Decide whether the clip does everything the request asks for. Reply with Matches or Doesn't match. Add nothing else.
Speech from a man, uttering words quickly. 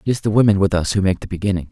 Matches